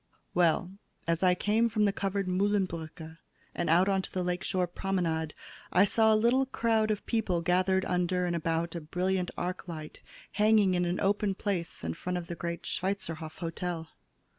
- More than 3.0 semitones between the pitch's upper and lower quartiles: No, average, 2.7 semitones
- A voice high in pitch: No, medium, 180 Hz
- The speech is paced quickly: No, average, 175 wpm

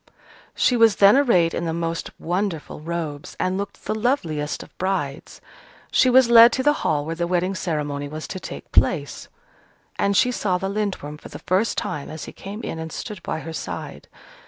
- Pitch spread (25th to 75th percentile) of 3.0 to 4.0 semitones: No, average, 4.9 semitones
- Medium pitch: Yes, medium, 180 Hz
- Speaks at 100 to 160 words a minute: No, average, 195 wpm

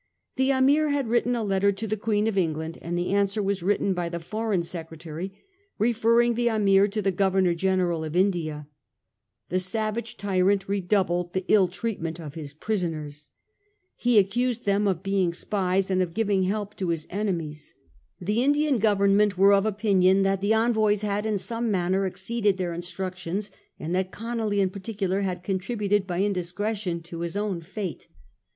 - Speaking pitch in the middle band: No, high, 195 Hz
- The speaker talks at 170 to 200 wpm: Yes, average, 175 wpm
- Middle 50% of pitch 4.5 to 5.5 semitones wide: No, average, 3.1 semitones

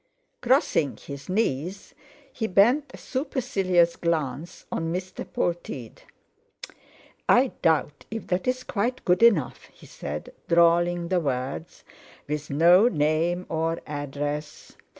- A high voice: No, medium, 170 Hz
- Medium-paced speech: No, slow, 110 wpm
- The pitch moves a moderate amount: Yes, average, 5.0 semitones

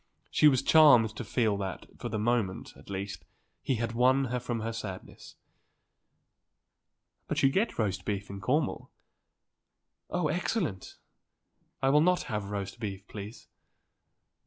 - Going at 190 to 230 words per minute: No, average, 140 wpm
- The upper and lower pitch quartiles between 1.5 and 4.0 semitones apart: No, average, 5.1 semitones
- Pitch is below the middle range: Yes, low, 115 Hz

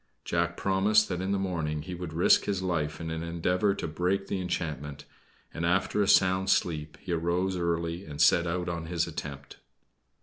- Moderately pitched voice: No, very low, 85 Hz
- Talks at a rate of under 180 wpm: No, average, 190 wpm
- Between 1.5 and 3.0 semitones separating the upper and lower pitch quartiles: Yes, narrow, 2.5 semitones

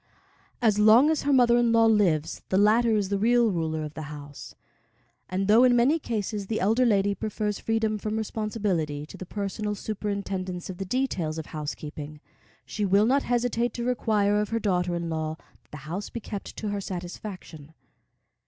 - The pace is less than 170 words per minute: No, average, 185 wpm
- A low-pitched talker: No, high, 205 Hz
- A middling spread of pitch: Yes, average, 4.2 semitones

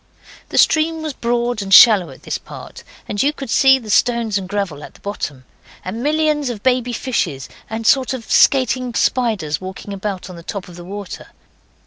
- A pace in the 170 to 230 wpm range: Yes, average, 195 wpm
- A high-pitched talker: Yes, high, 225 Hz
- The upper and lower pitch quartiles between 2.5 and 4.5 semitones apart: No, average, 5.0 semitones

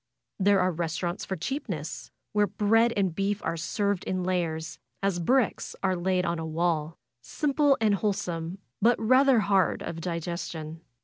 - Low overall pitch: No, medium, 185 Hz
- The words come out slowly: No, average, 165 wpm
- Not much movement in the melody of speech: No, average, 3.7 semitones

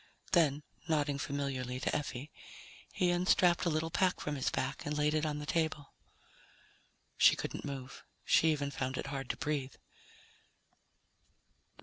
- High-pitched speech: No, medium, 145 Hz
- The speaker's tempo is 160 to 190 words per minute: No, average, 145 wpm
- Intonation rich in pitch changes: No, narrow, 2.4 semitones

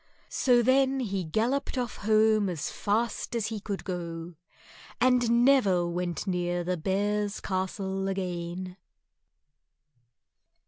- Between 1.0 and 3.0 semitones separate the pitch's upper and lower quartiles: No, average, 4.4 semitones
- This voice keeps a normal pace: No, slow, 110 wpm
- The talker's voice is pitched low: No, high, 195 Hz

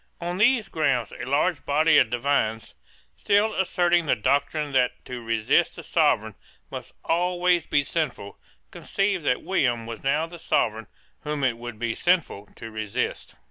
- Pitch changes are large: Yes, wide, 6.6 semitones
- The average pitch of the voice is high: No, medium, 145 Hz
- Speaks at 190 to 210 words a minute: No, average, 155 wpm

